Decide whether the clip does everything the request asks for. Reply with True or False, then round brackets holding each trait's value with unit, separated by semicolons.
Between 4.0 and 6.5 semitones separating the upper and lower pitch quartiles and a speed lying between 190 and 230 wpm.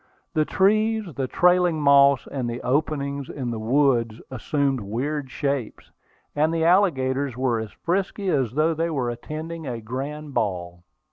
False (4.3 semitones; 150 wpm)